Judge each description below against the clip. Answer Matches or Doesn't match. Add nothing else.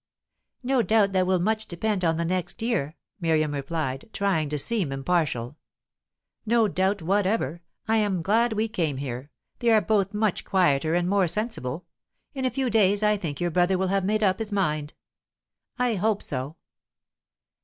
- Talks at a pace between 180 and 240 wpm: Doesn't match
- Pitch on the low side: Doesn't match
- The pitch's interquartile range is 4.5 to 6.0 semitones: Matches